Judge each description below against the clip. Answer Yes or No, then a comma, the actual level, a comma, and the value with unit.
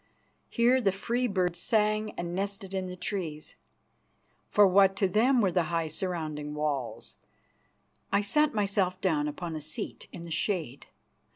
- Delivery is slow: No, average, 155 wpm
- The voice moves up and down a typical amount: Yes, average, 4.0 semitones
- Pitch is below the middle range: No, medium, 185 Hz